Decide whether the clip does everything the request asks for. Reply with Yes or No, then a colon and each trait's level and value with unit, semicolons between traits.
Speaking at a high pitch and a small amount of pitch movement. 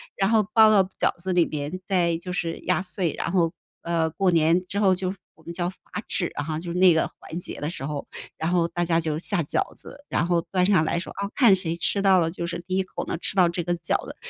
No: medium, 175 Hz; narrow, 2.2 semitones